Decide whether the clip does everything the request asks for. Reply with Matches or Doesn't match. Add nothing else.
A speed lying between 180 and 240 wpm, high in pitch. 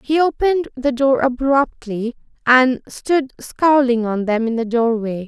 Doesn't match